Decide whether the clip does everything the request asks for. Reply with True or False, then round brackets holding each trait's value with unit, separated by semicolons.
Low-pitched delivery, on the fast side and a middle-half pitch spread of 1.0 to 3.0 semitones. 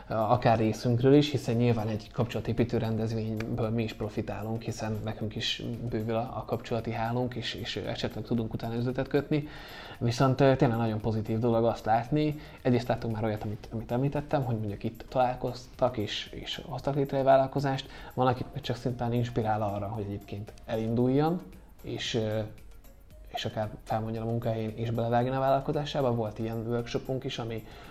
True (115 Hz; 160 wpm; 2.5 semitones)